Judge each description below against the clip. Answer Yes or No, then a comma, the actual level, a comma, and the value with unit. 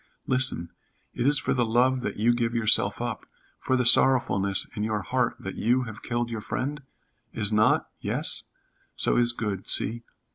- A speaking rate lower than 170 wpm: No, average, 175 wpm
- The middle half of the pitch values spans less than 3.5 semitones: Yes, average, 2.9 semitones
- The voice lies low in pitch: Yes, low, 120 Hz